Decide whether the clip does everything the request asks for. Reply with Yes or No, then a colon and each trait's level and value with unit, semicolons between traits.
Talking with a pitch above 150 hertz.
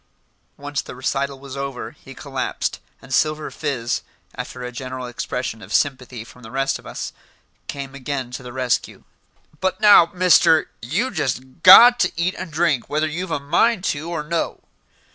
No: medium, 140 Hz